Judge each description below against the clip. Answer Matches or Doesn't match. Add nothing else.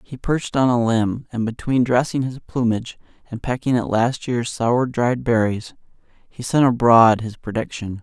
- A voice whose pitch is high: Doesn't match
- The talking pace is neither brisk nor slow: Matches